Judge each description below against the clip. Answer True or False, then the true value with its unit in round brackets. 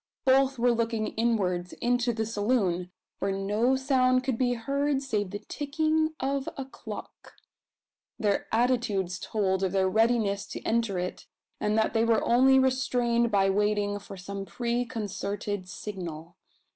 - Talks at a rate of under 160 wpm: True (145 wpm)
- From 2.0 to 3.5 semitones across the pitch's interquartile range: False (4.2 semitones)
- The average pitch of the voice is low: False (225 Hz)